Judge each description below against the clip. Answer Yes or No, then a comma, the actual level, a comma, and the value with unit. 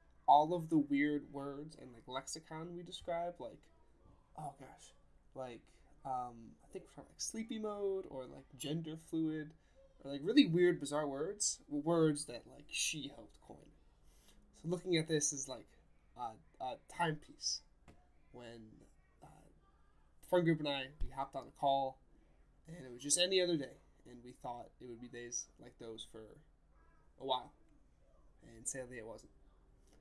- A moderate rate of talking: Yes, average, 160 wpm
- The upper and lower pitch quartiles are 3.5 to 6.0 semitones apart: Yes, average, 4.8 semitones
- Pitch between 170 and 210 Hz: No, medium, 145 Hz